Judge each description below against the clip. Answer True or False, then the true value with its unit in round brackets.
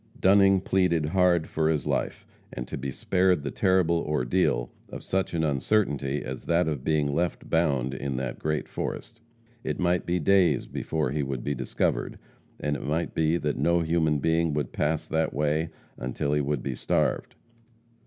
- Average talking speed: True (175 wpm)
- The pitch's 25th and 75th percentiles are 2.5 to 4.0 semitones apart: True (3.3 semitones)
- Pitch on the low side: True (80 Hz)